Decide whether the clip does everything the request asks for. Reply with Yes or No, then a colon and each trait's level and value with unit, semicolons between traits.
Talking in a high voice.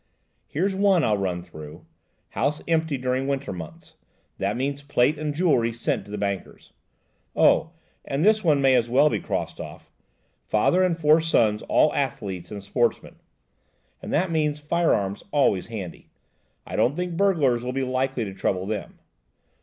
No: low, 135 Hz